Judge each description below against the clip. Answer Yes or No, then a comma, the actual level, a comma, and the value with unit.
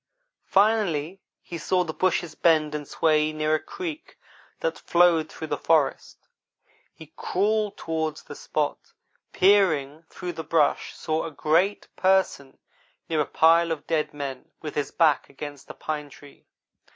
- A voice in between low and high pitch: Yes, medium, 160 Hz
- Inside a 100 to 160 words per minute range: Yes, average, 150 wpm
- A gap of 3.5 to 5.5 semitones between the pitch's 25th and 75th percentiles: No, average, 3.1 semitones